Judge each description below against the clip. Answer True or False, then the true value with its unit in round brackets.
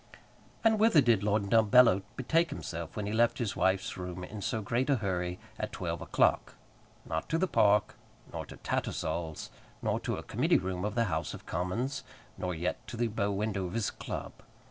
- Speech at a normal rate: True (190 wpm)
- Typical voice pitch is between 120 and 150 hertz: False (105 Hz)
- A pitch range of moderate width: True (4.6 semitones)